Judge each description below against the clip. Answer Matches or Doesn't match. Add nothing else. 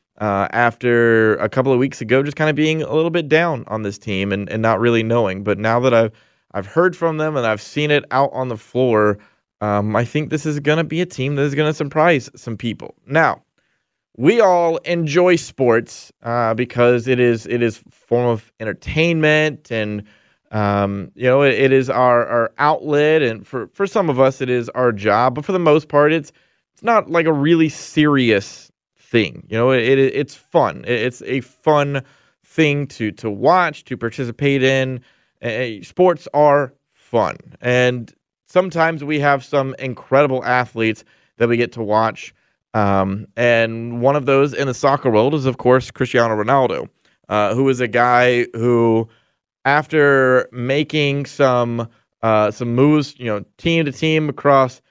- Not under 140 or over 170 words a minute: Doesn't match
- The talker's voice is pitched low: Matches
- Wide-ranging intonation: Doesn't match